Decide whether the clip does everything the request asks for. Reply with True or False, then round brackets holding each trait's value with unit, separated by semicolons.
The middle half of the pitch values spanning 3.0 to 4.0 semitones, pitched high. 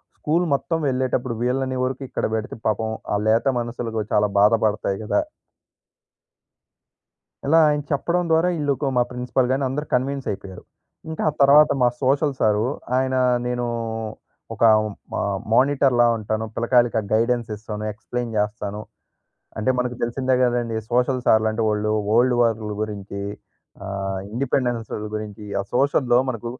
False (3.3 semitones; 120 Hz)